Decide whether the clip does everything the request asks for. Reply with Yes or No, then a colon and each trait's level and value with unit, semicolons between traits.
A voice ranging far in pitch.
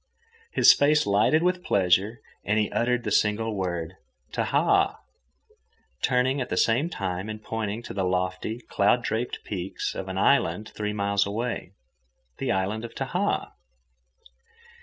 No: average, 3.9 semitones